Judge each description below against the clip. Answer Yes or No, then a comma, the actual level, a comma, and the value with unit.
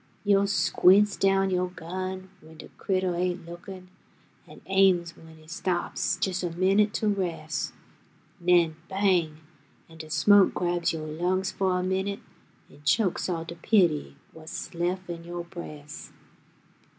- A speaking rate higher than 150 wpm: No, average, 145 wpm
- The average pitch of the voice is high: No, medium, 180 Hz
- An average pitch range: No, narrow, 2.3 semitones